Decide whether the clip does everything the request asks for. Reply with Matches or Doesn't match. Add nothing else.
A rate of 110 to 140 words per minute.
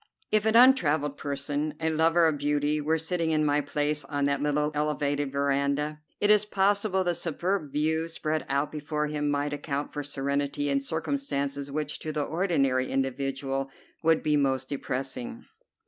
Doesn't match